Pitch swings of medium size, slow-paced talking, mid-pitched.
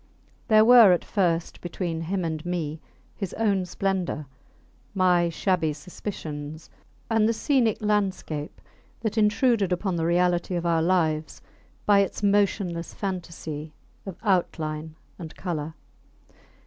Yes: average, 3.7 semitones; slow, 120 wpm; medium, 180 Hz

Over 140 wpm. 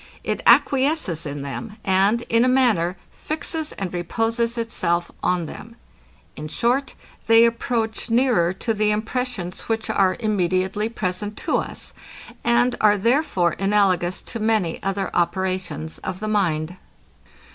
No: slow, 135 wpm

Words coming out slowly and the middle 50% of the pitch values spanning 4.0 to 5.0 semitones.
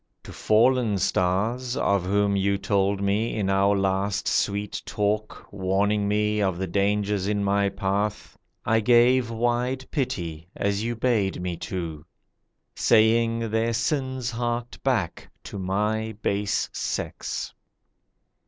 No: slow, 125 wpm; average, 2.8 semitones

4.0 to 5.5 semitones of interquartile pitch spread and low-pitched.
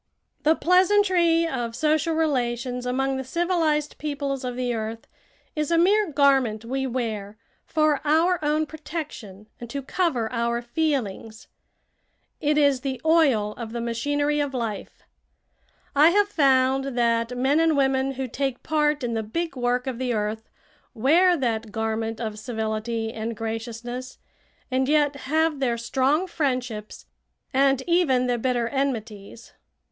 No: average, 4.5 semitones; very high, 265 Hz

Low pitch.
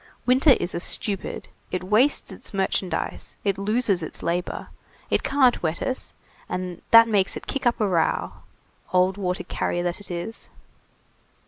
No: high, 195 Hz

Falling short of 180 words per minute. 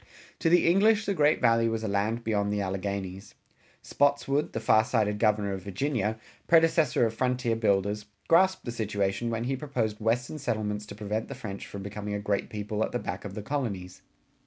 No: average, 190 wpm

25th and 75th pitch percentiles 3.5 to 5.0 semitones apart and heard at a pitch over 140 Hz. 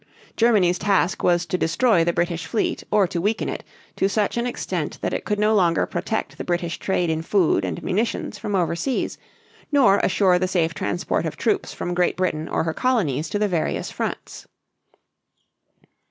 Yes: average, 3.8 semitones; medium, 185 Hz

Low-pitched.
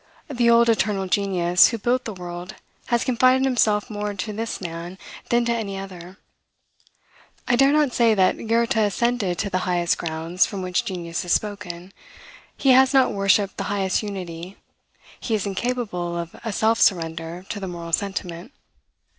No: high, 200 Hz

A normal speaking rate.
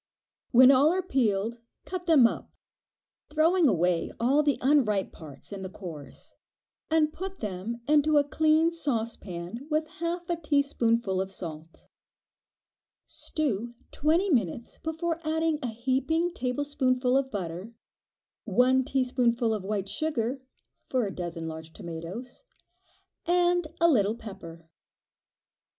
No: slow, 120 wpm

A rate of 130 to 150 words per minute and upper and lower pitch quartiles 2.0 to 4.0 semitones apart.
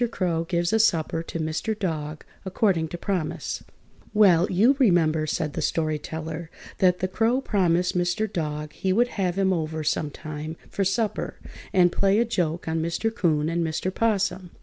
No: average, 170 wpm; average, 3.5 semitones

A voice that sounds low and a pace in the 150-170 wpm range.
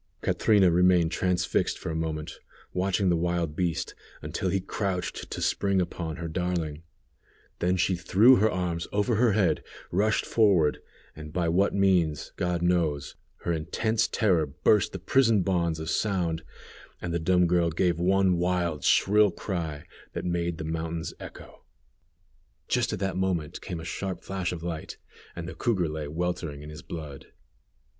Yes: very low, 90 Hz; average, 160 wpm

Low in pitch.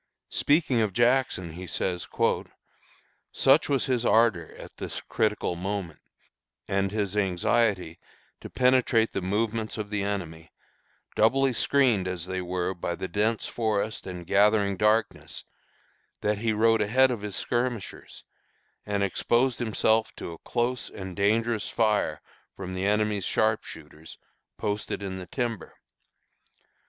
Yes: low, 105 Hz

